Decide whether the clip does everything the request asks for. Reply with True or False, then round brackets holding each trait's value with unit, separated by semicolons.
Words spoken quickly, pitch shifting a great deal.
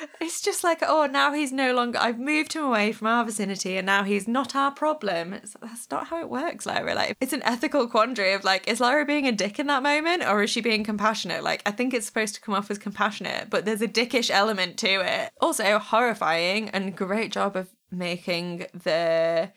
True (225 wpm; 6.0 semitones)